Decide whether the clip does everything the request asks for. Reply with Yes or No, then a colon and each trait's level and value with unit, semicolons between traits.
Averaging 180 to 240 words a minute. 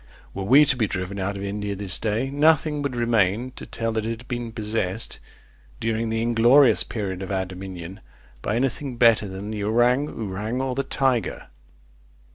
Yes: average, 185 wpm